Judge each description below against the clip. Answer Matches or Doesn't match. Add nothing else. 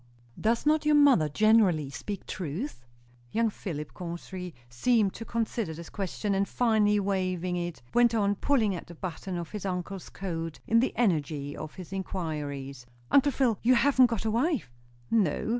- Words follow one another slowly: Doesn't match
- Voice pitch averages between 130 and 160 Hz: Doesn't match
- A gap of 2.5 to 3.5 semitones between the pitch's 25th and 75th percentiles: Doesn't match